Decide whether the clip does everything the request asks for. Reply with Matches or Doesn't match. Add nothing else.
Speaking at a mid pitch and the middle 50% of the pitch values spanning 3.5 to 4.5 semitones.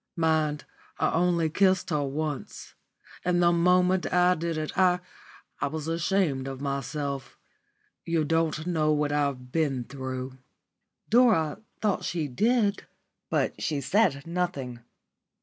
Matches